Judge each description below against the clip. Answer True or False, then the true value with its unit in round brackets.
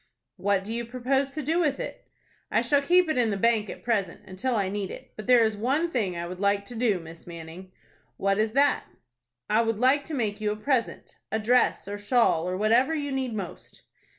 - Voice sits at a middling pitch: False (225 Hz)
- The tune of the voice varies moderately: True (4.7 semitones)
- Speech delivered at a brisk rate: True (220 wpm)